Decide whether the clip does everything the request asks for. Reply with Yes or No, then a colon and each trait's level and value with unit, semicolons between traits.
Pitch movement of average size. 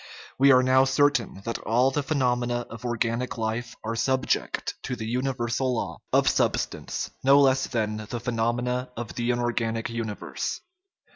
No: narrow, 2.1 semitones